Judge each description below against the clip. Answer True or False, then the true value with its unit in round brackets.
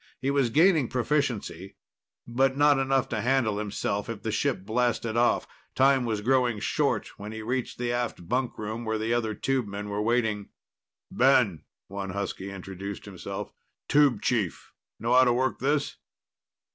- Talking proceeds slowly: False (155 wpm)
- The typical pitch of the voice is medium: False (120 Hz)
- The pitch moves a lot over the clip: False (4.2 semitones)